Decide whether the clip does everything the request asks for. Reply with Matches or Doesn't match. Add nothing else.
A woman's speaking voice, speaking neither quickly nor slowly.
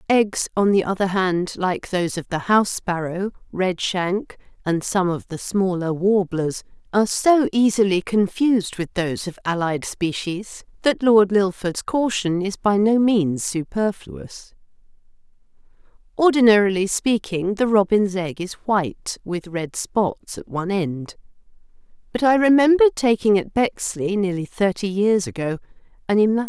Matches